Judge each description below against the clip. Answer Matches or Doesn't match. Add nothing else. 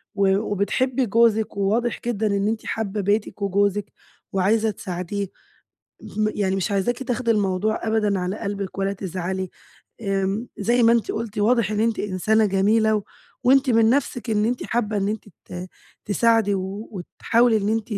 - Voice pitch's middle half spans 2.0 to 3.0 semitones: Matches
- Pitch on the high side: Matches